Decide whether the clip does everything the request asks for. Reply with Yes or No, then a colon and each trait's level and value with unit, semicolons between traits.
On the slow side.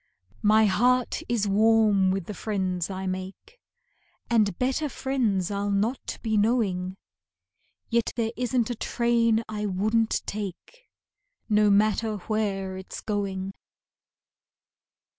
Yes: slow, 115 wpm